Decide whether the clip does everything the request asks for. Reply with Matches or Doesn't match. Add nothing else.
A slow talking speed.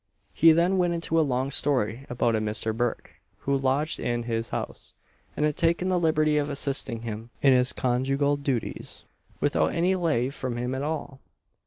Doesn't match